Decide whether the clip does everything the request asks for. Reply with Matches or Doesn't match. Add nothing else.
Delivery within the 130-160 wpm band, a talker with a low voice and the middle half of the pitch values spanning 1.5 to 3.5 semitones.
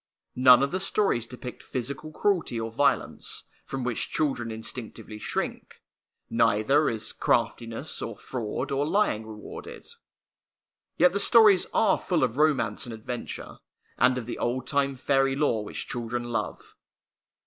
Doesn't match